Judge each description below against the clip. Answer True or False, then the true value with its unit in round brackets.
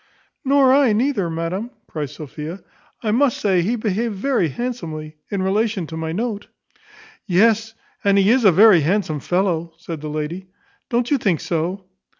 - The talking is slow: False (160 wpm)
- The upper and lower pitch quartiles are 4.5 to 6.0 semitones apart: True (5.4 semitones)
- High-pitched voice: True (195 Hz)